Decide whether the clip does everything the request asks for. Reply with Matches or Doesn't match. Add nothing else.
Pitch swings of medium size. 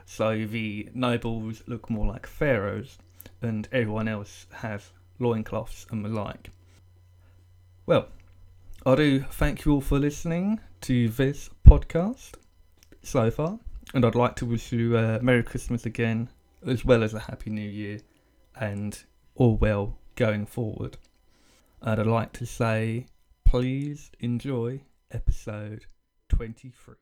Matches